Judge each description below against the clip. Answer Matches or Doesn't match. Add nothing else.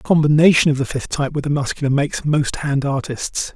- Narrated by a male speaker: Matches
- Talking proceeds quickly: Matches